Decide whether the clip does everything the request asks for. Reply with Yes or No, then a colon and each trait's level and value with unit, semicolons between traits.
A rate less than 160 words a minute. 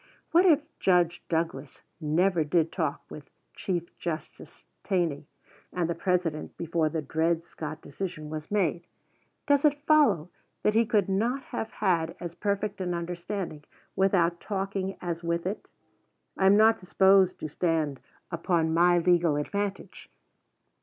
Yes: average, 140 wpm